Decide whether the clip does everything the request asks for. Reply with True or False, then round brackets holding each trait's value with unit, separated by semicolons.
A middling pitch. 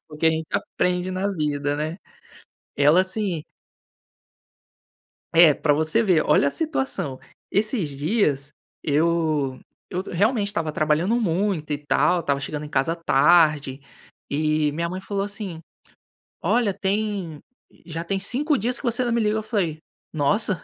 True (170 Hz)